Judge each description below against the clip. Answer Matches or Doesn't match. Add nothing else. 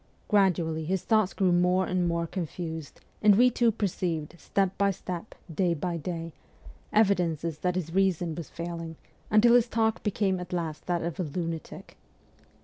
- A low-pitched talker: Doesn't match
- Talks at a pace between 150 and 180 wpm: Matches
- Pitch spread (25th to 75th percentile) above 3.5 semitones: Doesn't match